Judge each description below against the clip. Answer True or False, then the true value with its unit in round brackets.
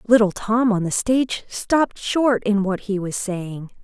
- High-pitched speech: True (210 Hz)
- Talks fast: False (190 wpm)